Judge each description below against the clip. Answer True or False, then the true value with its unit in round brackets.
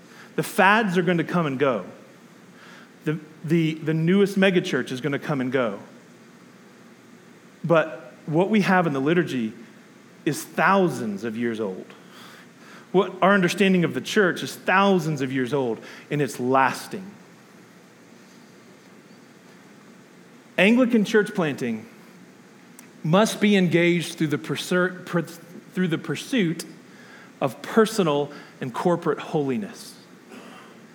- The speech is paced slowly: True (120 wpm)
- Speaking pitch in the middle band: True (180 Hz)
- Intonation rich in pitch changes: False (4.4 semitones)